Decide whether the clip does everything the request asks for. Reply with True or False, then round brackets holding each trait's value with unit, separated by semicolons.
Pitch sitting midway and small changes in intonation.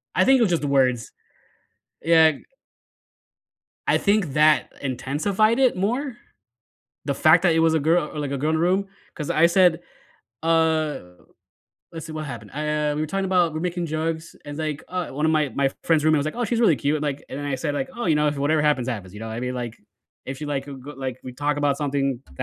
False (150 Hz; 3.0 semitones)